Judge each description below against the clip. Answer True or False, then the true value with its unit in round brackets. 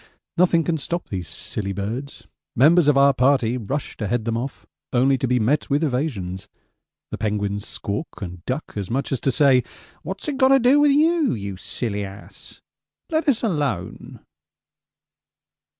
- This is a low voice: True (130 Hz)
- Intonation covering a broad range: True (7.5 semitones)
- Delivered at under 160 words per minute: False (165 wpm)